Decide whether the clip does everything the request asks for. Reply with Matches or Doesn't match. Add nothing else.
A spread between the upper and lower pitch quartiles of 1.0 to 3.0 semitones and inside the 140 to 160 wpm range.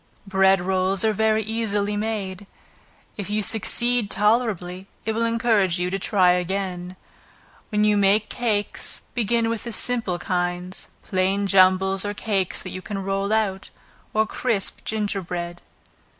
Matches